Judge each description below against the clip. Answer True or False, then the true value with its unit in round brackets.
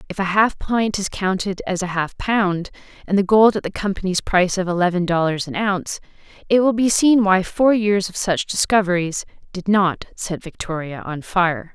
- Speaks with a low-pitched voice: False (190 Hz)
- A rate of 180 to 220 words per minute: True (195 wpm)